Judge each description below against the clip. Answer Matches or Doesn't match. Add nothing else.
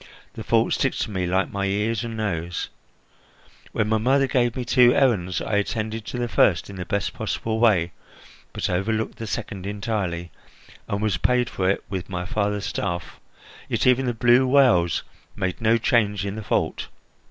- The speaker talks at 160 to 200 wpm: Matches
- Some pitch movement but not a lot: Matches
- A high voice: Doesn't match